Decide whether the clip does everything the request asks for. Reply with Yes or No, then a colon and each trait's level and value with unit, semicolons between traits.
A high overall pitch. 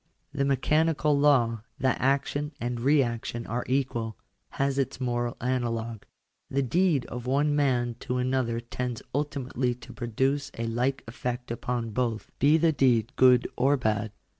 No: low, 125 Hz